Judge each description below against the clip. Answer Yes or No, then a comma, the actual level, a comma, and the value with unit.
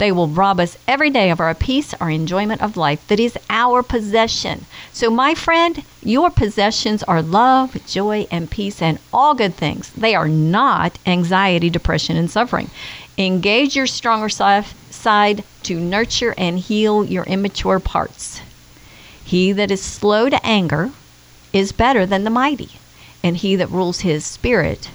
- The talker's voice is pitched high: Yes, high, 200 Hz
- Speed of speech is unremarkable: Yes, average, 160 wpm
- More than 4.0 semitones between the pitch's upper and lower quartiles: Yes, average, 4.6 semitones